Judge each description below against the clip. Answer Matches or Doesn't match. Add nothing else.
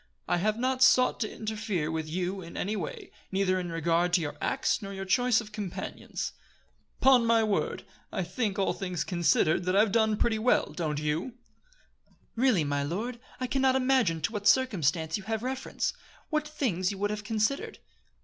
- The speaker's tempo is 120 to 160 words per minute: Doesn't match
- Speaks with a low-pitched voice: Doesn't match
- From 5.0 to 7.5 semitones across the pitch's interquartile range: Matches